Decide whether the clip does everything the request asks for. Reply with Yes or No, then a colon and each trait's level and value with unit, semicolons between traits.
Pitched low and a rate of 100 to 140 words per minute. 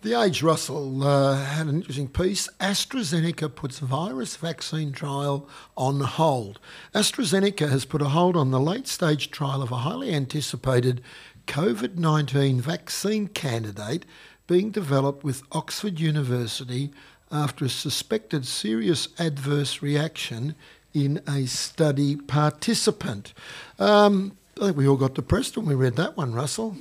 No: medium, 150 Hz; slow, 135 wpm